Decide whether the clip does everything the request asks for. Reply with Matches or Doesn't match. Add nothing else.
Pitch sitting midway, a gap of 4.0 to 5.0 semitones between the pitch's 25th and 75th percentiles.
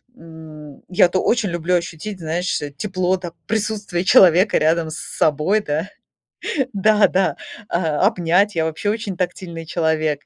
Doesn't match